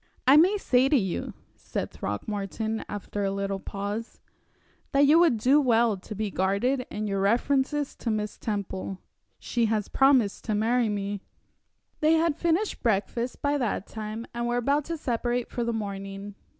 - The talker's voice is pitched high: Yes, high, 225 Hz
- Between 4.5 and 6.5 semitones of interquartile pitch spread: Yes, average, 4.8 semitones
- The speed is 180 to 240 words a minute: No, average, 165 wpm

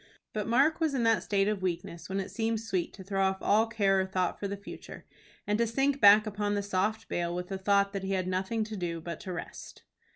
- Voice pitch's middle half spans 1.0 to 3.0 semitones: Yes, narrow, 2.6 semitones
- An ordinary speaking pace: No, fast, 250 wpm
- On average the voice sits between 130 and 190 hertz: No, high, 200 Hz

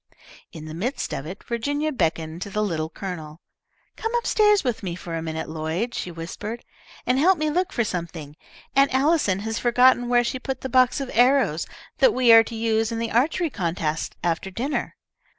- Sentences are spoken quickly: No, average, 195 wpm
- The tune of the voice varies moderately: No, wide, 7.6 semitones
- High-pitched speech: Yes, high, 225 Hz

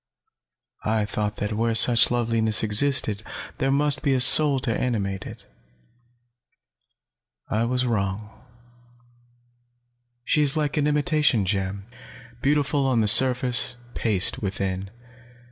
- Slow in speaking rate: Yes, slow, 115 wpm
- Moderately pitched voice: No, low, 115 Hz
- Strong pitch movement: No, average, 4.7 semitones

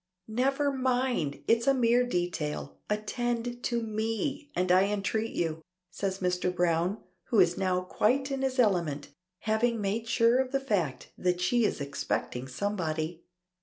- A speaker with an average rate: Yes, average, 150 wpm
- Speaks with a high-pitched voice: Yes, high, 210 Hz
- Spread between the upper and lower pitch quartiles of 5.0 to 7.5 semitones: Yes, wide, 5.5 semitones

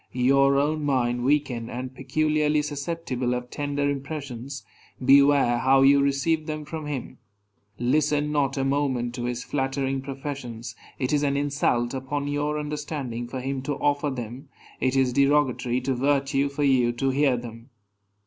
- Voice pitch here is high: No, low, 135 Hz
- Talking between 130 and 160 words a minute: Yes, average, 155 wpm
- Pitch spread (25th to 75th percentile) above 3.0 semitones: No, narrow, 2.4 semitones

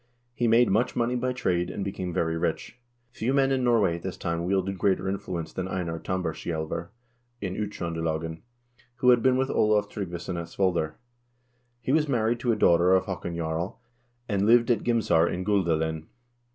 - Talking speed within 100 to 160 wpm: No, average, 175 wpm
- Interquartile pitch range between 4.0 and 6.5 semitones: Yes, wide, 5.5 semitones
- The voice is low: Yes, very low, 95 Hz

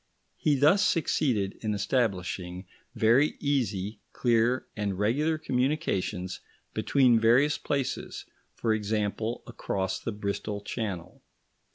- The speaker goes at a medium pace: No, slow, 100 wpm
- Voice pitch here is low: Yes, low, 110 Hz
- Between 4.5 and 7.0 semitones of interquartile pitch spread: Yes, average, 4.9 semitones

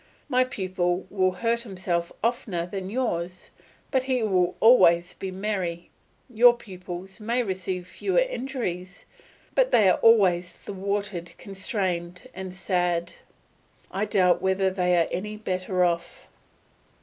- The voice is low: No, high, 190 Hz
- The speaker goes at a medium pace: No, slow, 125 wpm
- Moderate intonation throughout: Yes, average, 3.5 semitones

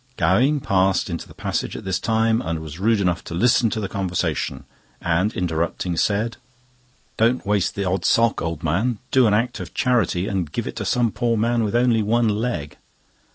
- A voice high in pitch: No, low, 105 Hz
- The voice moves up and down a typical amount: Yes, average, 4.7 semitones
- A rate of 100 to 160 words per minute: No, average, 195 wpm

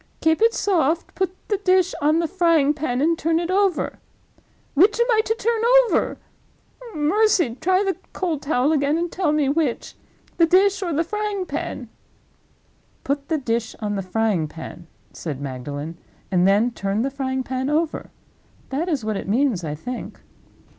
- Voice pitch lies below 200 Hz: No, very high, 300 Hz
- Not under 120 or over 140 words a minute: No, average, 165 wpm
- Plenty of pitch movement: Yes, wide, 7.6 semitones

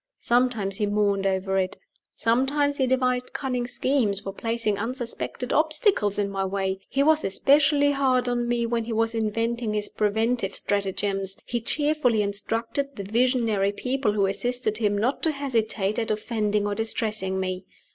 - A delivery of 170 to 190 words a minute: No, average, 155 wpm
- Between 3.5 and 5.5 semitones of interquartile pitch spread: Yes, average, 3.8 semitones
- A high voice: Yes, high, 225 Hz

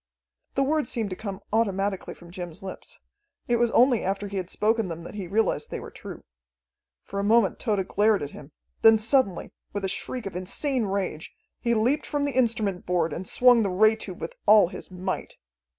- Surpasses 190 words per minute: Yes, average, 200 wpm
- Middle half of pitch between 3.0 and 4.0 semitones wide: Yes, average, 3.7 semitones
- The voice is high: Yes, high, 205 Hz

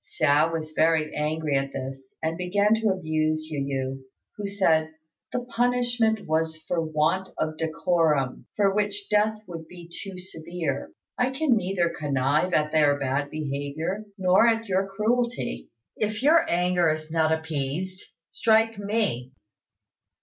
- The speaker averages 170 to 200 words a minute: No, average, 140 wpm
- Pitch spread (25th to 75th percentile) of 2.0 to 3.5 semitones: No, average, 4.9 semitones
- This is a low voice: No, medium, 165 Hz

